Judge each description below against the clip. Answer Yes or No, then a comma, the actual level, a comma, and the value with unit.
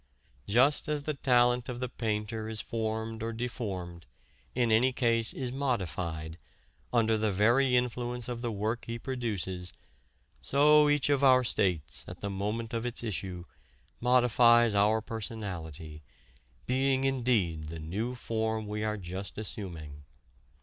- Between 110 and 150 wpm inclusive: Yes, average, 140 wpm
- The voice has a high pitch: No, low, 115 Hz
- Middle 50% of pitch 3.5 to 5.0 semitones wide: Yes, average, 3.9 semitones